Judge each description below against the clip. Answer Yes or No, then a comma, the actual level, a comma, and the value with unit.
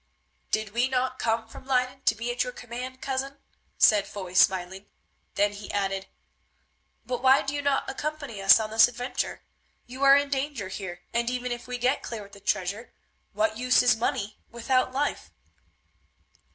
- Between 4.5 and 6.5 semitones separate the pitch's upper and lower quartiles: No, average, 4.0 semitones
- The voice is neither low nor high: No, high, 245 Hz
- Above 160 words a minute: Yes, average, 175 wpm